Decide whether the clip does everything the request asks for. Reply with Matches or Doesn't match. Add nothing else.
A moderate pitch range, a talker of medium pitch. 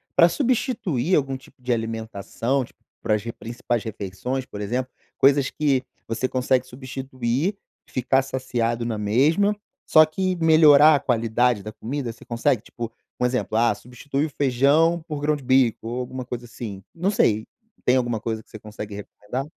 Doesn't match